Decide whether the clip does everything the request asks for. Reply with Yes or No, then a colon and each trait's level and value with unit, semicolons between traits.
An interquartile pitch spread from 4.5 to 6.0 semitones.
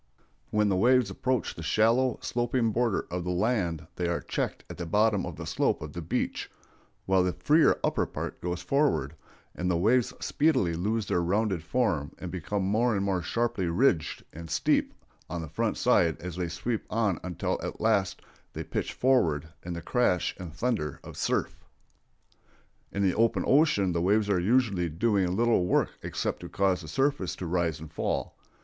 Yes: average, 5.0 semitones